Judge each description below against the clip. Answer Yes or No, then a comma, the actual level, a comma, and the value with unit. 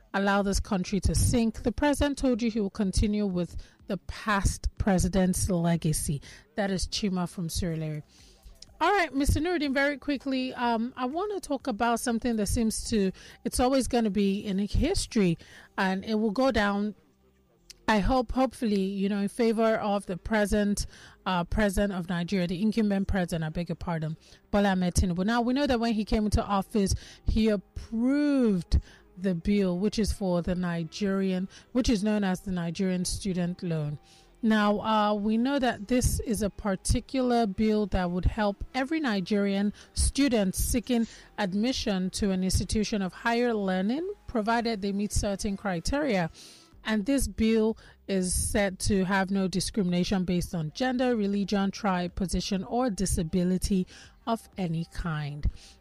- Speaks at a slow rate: No, average, 155 wpm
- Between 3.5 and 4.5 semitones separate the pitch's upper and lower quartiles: Yes, average, 3.8 semitones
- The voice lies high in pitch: Yes, high, 205 Hz